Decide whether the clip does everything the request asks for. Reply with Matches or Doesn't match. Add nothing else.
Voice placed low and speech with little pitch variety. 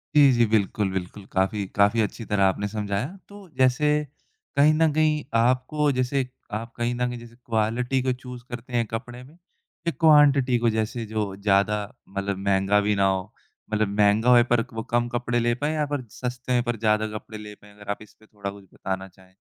Doesn't match